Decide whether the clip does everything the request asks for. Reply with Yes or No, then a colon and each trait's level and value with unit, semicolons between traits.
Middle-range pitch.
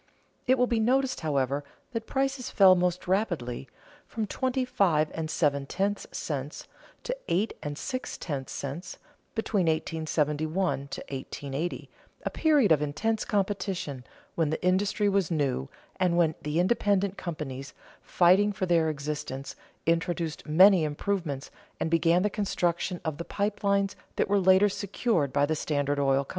Yes: medium, 175 Hz